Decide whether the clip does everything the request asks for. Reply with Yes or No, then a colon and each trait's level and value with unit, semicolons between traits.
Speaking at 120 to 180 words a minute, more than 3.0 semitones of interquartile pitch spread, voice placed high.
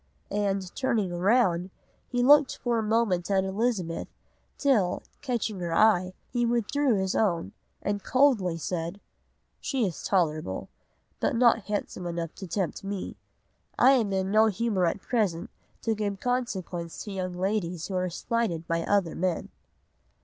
Yes: average, 150 wpm; average, 4.5 semitones; high, 195 Hz